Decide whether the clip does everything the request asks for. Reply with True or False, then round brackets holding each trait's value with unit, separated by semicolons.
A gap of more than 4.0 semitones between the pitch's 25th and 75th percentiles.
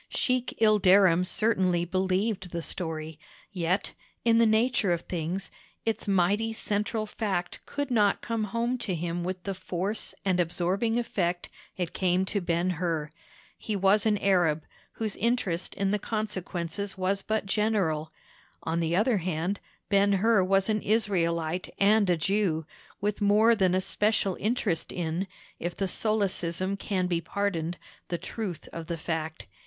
False (3.4 semitones)